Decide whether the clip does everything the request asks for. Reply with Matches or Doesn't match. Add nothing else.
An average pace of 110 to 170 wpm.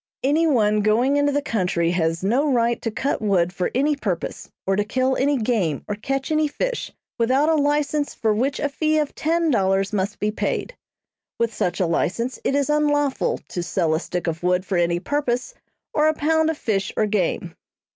Doesn't match